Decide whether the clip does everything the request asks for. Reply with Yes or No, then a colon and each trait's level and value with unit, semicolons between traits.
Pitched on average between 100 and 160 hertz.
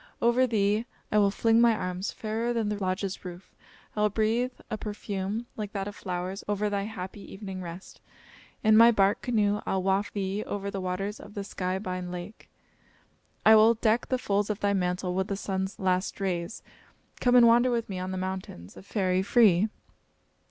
No: high, 200 Hz